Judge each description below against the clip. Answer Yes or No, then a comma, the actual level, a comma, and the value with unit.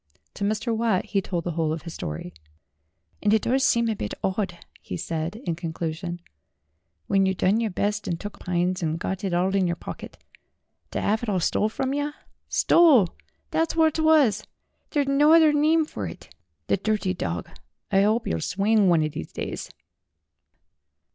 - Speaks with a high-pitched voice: Yes, high, 200 Hz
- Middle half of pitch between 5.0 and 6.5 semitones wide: Yes, average, 5.3 semitones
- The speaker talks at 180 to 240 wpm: Yes, average, 185 wpm